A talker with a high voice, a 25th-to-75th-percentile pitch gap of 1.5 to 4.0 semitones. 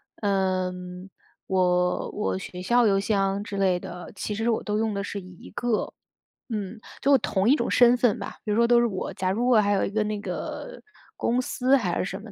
Yes: high, 205 Hz; average, 3.5 semitones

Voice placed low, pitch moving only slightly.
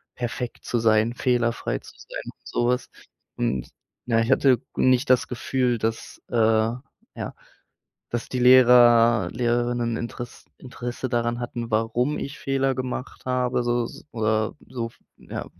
Yes: low, 120 Hz; narrow, 1.5 semitones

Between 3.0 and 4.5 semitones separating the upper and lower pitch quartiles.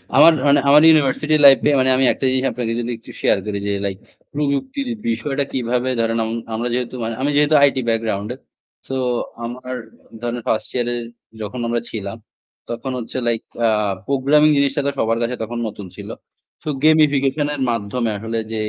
Yes: average, 3.7 semitones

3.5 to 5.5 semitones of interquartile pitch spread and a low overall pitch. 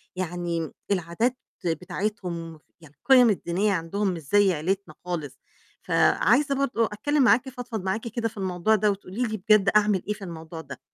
No: average, 4.4 semitones; high, 200 Hz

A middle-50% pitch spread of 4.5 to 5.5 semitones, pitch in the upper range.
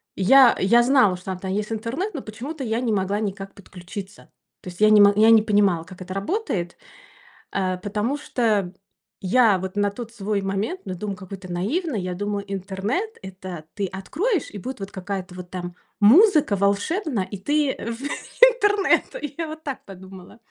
Yes: average, 5.2 semitones; high, 205 Hz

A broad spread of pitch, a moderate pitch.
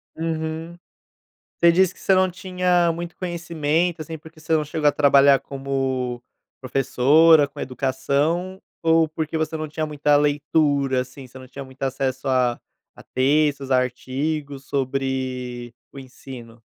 No: average, 3.5 semitones; medium, 145 Hz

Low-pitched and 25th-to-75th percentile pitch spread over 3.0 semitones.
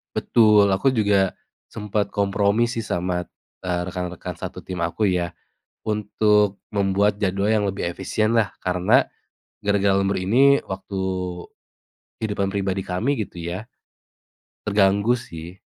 No: low, 100 Hz; narrow, 2.4 semitones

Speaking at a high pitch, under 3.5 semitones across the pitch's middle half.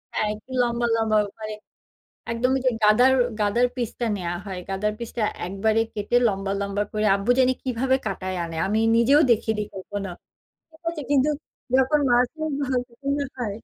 No: high, 230 Hz; average, 3.9 semitones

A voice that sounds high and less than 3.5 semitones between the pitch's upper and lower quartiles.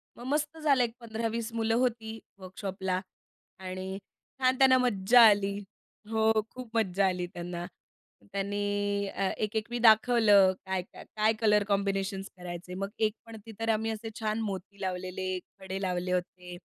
Yes: high, 205 Hz; average, 3.1 semitones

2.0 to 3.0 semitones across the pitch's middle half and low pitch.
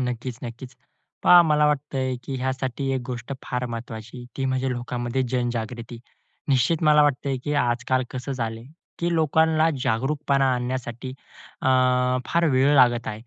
Yes: narrow, 2.5 semitones; low, 130 Hz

